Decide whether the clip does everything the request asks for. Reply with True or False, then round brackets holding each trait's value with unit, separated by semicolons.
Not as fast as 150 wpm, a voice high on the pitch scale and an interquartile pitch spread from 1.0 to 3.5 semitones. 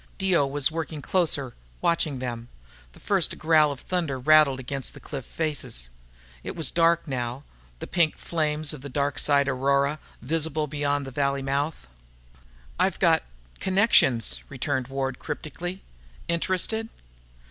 False (135 wpm; 145 Hz; 3.2 semitones)